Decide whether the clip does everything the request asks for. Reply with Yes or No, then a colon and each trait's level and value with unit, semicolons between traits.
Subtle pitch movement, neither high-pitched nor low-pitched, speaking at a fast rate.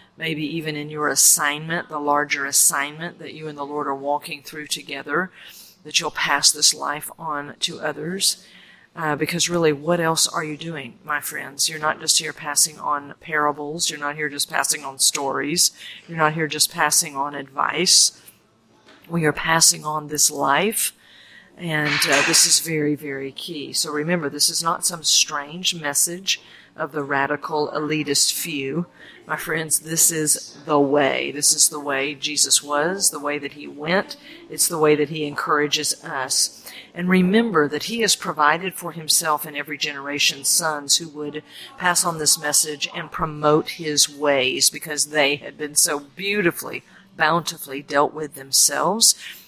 No: narrow, 2.0 semitones; medium, 150 Hz; average, 165 wpm